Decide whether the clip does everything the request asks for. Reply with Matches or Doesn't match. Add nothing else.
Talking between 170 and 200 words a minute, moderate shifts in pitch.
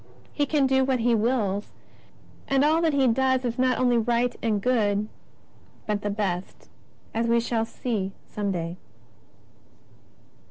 Doesn't match